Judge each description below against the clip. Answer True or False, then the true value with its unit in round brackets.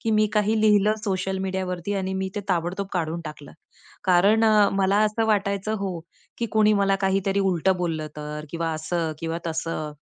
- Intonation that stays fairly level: False (3.3 semitones)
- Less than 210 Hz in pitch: True (190 Hz)